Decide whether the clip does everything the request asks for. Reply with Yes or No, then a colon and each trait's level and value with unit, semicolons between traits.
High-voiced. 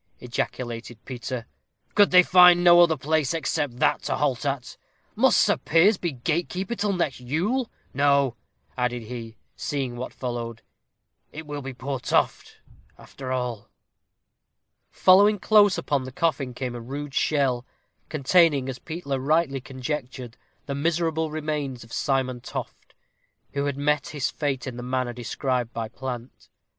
No: medium, 140 Hz